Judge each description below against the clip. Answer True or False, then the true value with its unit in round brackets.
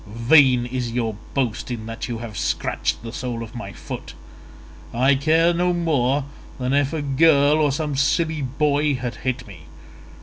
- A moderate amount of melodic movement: True (3.7 semitones)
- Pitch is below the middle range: True (130 Hz)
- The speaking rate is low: False (170 wpm)